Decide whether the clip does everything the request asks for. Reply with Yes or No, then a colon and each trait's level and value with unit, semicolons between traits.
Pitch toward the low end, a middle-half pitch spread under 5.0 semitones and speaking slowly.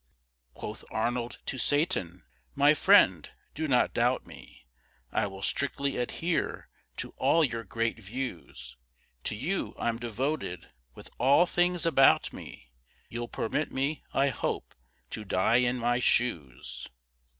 Yes: low, 125 Hz; average, 4.1 semitones; slow, 130 wpm